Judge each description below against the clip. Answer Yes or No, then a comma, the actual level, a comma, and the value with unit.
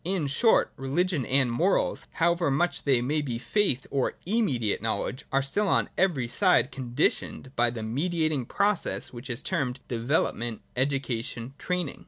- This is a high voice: No, low, 135 Hz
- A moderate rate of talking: Yes, average, 150 wpm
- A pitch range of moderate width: No, wide, 6.0 semitones